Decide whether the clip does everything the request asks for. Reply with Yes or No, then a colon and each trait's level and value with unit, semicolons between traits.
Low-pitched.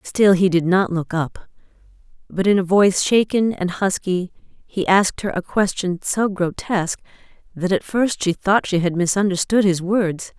No: high, 190 Hz